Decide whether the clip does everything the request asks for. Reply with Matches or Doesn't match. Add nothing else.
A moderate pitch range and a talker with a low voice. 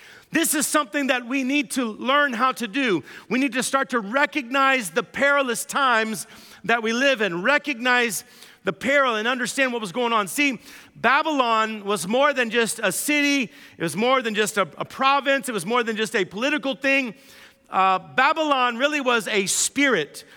Doesn't match